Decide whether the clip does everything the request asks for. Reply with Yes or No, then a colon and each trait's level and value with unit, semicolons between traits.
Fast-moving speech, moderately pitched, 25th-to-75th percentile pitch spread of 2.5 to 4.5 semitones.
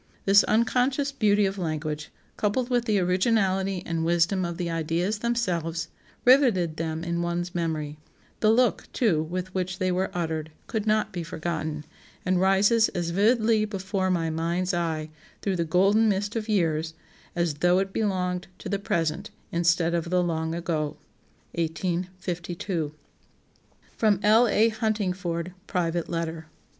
No: average, 145 wpm; medium, 180 Hz; average, 3.6 semitones